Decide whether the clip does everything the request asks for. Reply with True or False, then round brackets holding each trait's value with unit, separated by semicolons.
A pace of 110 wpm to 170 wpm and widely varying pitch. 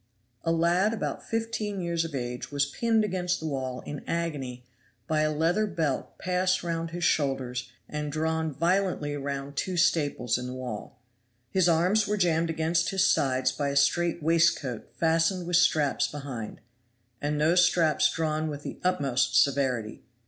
False (160 wpm; 3.8 semitones)